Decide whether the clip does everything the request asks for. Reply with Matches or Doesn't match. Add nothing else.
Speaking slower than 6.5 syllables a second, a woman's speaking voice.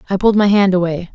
Doesn't match